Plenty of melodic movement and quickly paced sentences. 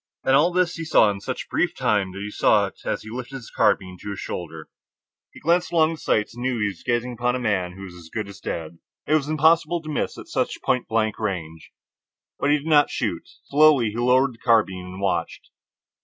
Yes: wide, 7.0 semitones; fast, 235 wpm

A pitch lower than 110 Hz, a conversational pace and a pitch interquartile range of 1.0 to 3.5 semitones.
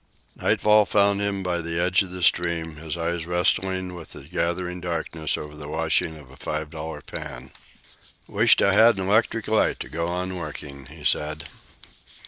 Yes: very low, 85 Hz; average, 175 wpm; average, 3.0 semitones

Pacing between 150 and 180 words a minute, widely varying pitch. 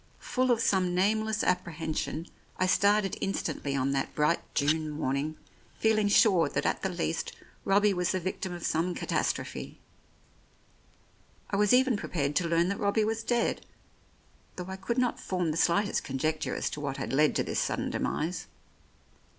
No: average, 175 wpm; average, 4.8 semitones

